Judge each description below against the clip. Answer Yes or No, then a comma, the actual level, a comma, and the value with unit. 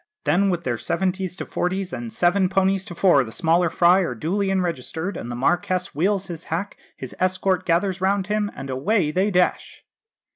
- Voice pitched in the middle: Yes, medium, 180 Hz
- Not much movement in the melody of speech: No, average, 3.0 semitones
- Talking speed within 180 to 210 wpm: Yes, average, 185 wpm